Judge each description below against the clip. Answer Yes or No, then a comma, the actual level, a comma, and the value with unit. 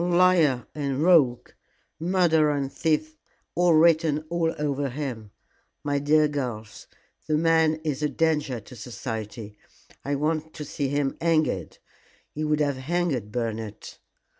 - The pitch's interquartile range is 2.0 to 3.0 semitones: No, average, 3.6 semitones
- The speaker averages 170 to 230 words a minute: No, slow, 135 wpm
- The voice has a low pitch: No, medium, 150 Hz